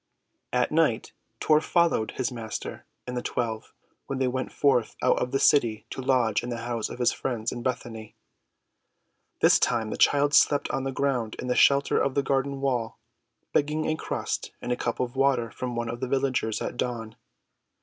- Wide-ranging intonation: No, average, 2.7 semitones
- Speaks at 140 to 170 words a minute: No, average, 190 wpm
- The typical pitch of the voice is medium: No, low, 125 Hz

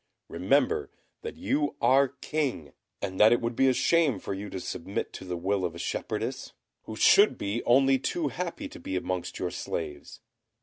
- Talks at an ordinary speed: Yes, average, 185 wpm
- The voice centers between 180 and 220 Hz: No, low, 135 Hz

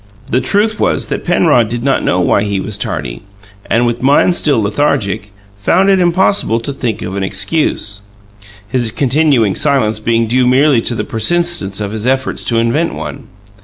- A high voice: No, low, 120 Hz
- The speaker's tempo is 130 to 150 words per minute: No, average, 175 wpm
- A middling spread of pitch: No, wide, 5.7 semitones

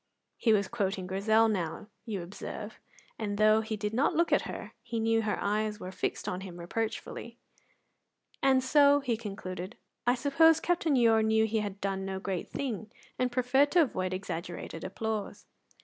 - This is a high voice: Yes, high, 220 Hz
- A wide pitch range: No, average, 3.8 semitones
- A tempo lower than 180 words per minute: Yes, average, 170 wpm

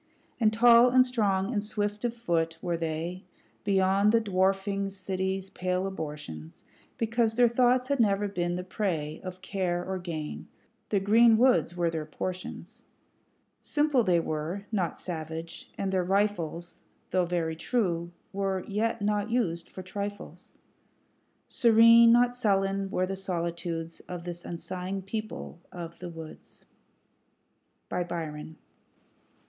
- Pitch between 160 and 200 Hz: Yes, high, 190 Hz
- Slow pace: Yes, slow, 130 wpm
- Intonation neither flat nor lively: Yes, average, 3.7 semitones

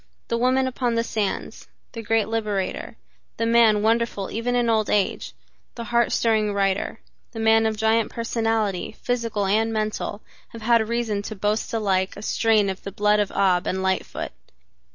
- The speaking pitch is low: No, high, 220 Hz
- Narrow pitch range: Yes, narrow, 2.0 semitones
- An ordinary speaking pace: Yes, average, 170 wpm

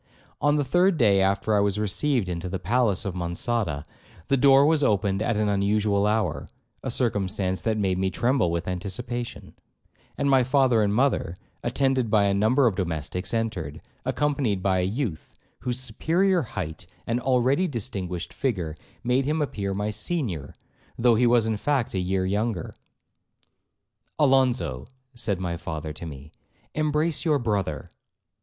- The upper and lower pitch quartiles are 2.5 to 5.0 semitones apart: No, wide, 5.6 semitones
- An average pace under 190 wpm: Yes, average, 155 wpm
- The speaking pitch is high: No, low, 110 Hz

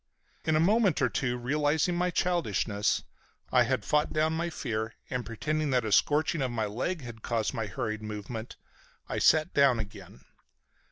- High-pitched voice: No, low, 130 Hz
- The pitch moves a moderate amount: No, wide, 6.0 semitones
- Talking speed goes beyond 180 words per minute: No, average, 170 wpm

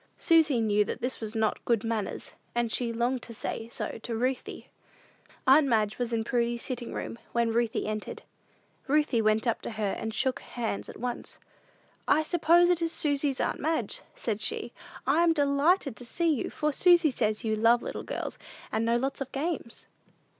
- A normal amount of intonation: Yes, average, 4.3 semitones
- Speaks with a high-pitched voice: Yes, high, 240 Hz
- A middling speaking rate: Yes, average, 185 wpm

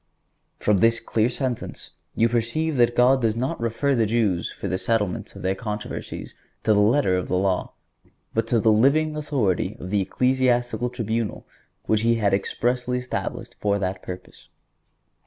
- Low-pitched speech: Yes, low, 115 Hz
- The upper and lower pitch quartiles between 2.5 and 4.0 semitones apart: Yes, average, 3.3 semitones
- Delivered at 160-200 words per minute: Yes, average, 170 wpm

